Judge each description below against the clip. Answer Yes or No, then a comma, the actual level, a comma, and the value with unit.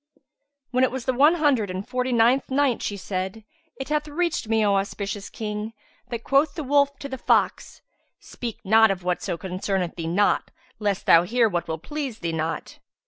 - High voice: Yes, high, 225 Hz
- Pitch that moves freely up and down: Yes, wide, 5.7 semitones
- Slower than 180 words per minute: No, average, 190 wpm